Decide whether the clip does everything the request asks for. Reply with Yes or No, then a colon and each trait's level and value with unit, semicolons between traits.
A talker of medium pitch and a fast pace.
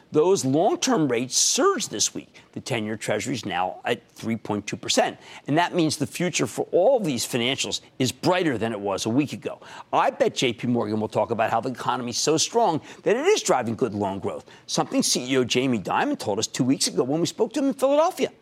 Yes: medium, 145 Hz; fast, 220 wpm